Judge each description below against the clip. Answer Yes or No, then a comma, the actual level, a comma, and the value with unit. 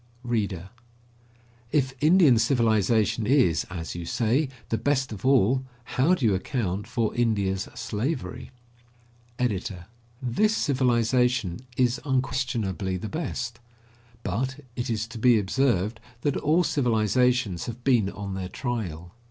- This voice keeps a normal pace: No, slow, 125 wpm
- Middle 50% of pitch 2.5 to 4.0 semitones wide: No, average, 4.6 semitones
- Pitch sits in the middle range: No, low, 120 Hz